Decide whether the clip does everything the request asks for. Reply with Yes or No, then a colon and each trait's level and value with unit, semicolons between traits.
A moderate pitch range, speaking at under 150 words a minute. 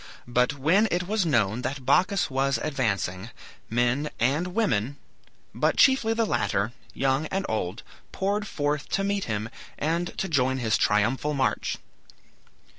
No: wide, 7.1 semitones; average, 140 wpm